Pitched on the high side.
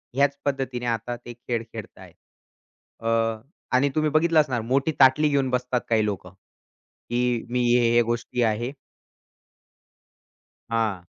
No: low, 125 Hz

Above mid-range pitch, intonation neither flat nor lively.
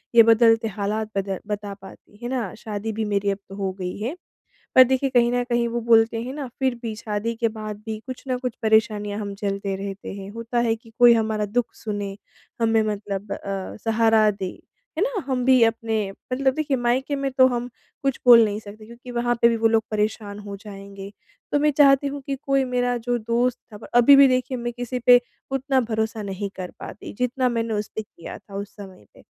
Yes: high, 225 Hz; average, 3.1 semitones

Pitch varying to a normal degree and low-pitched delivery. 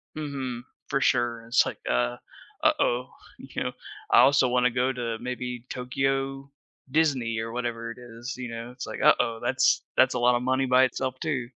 No: narrow, 1.8 semitones; low, 125 Hz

